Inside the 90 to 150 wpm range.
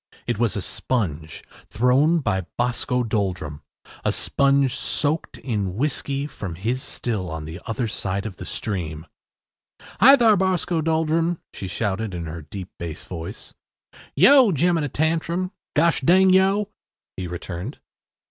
Yes: average, 140 wpm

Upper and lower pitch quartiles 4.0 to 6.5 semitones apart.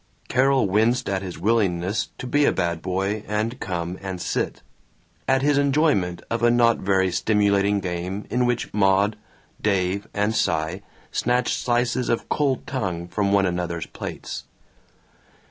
Yes: average, 4.6 semitones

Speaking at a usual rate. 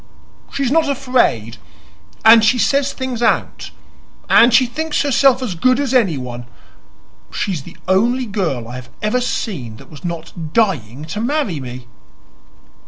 Yes: average, 150 wpm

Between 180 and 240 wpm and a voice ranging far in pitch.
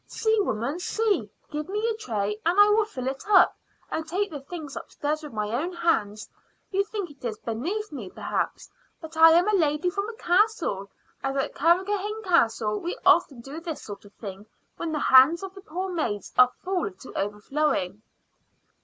Yes: average, 190 wpm; wide, 8.2 semitones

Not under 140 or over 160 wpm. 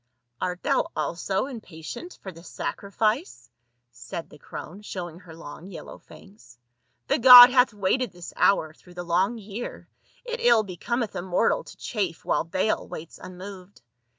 Yes: average, 155 wpm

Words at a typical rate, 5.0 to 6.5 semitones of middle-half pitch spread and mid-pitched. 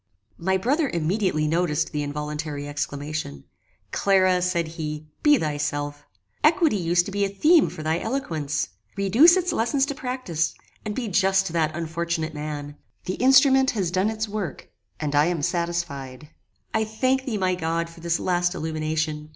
Yes: average, 160 wpm; wide, 5.6 semitones; medium, 170 Hz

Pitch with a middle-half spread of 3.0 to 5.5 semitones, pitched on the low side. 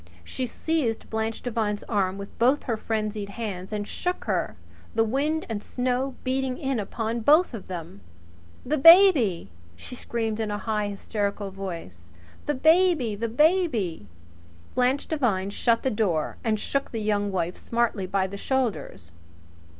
No: average, 4.5 semitones; high, 220 Hz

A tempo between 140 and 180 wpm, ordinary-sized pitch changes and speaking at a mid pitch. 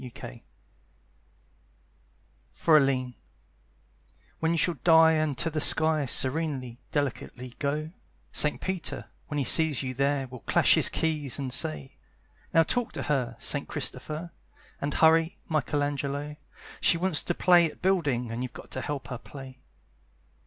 Yes: average, 145 wpm; average, 3.6 semitones; medium, 145 Hz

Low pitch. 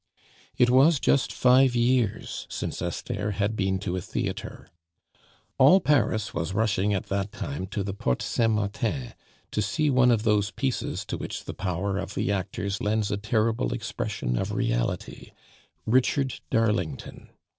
Yes: low, 105 Hz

